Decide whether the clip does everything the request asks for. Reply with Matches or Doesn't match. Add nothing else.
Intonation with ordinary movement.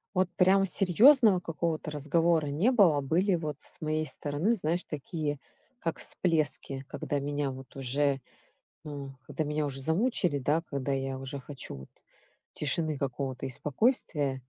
Matches